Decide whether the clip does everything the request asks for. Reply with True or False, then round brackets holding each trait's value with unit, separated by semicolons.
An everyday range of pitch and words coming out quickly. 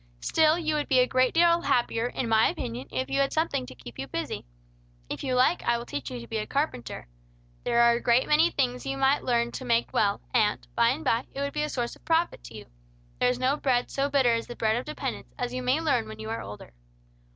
True (4.1 semitones; 255 wpm)